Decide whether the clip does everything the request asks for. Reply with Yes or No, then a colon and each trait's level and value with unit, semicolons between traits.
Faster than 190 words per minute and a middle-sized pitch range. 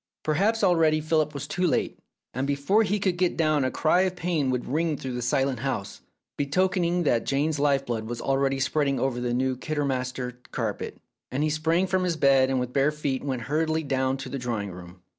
Yes: fast, 205 wpm; average, 3.8 semitones